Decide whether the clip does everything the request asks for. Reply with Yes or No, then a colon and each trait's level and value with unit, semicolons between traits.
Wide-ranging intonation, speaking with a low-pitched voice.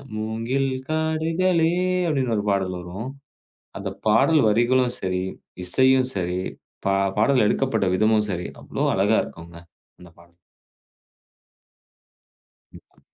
Yes: wide, 6.1 semitones; low, 110 Hz